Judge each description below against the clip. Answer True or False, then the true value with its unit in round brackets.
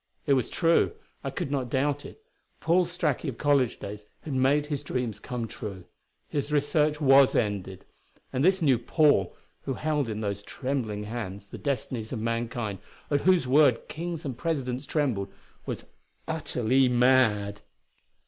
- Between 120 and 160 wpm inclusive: True (155 wpm)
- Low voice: True (130 Hz)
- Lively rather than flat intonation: False (4.8 semitones)